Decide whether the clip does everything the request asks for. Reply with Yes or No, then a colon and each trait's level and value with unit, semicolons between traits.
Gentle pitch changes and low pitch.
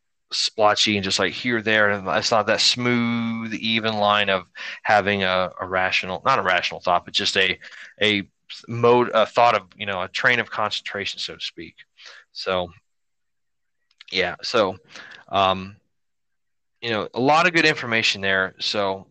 No: average, 3.4 semitones; low, 105 Hz